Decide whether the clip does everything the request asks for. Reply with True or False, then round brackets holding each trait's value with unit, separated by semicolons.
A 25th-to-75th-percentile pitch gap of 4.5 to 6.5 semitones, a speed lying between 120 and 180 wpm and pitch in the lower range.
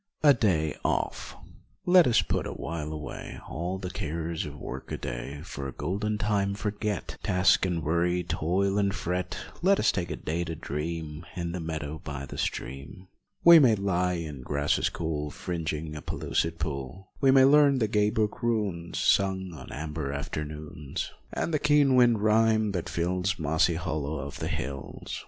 True (5.2 semitones; 175 wpm; 85 Hz)